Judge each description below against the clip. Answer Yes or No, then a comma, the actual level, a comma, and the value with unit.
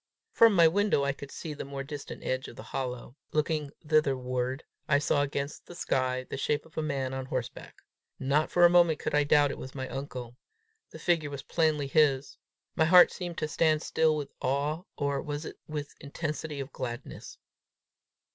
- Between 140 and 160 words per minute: No, average, 190 wpm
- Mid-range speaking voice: Yes, medium, 145 Hz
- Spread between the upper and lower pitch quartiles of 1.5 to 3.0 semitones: Yes, average, 2.7 semitones